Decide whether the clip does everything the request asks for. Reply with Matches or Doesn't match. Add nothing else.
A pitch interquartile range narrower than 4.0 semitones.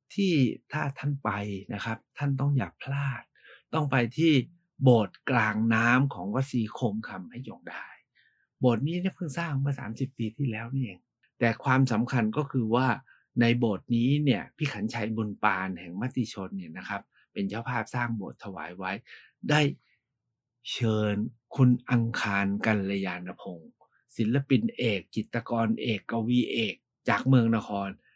Matches